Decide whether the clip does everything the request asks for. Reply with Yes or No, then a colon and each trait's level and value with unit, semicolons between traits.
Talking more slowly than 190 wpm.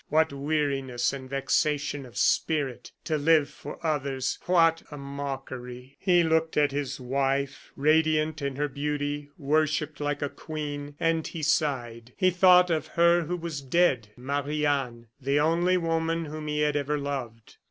Yes: average, 155 wpm